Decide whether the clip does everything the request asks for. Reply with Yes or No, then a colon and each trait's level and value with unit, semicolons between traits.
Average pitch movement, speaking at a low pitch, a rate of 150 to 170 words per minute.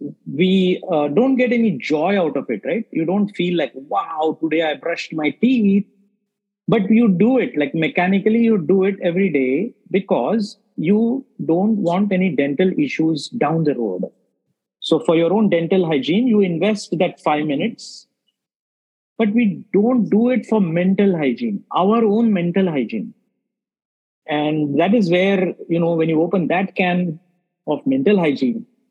No: average, 5.0 semitones; high, 190 Hz; average, 160 wpm